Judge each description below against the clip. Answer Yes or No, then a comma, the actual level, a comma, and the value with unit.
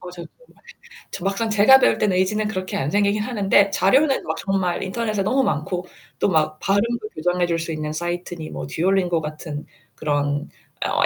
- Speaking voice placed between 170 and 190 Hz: Yes, medium, 185 Hz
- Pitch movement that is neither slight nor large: Yes, average, 4.0 semitones